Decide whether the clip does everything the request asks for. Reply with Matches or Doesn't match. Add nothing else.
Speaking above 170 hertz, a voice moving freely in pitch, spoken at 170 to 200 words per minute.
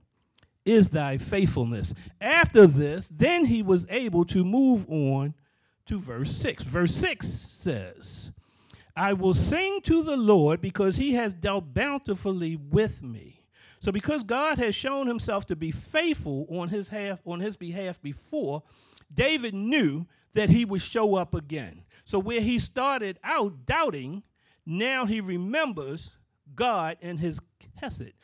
Doesn't match